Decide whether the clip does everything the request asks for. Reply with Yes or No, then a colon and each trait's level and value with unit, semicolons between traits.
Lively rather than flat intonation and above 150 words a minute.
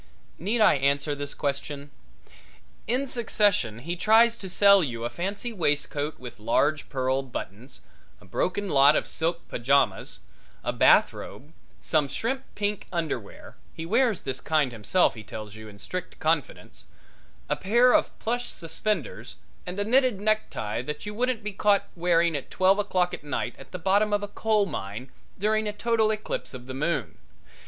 Yes: wide, 7.2 semitones; average, 165 wpm